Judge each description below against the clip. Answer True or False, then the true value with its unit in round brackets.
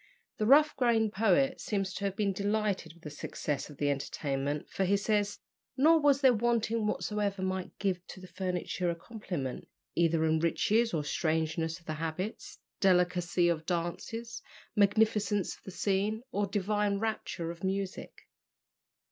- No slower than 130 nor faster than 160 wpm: True (155 wpm)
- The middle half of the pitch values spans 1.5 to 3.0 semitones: False (4.2 semitones)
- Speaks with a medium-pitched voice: False (195 Hz)